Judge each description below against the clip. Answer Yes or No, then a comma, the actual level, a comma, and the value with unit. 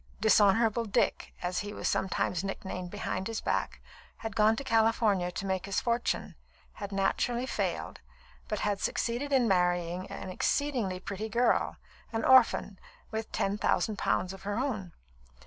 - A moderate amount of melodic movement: Yes, average, 3.1 semitones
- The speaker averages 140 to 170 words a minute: Yes, average, 150 wpm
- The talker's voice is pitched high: Yes, high, 205 Hz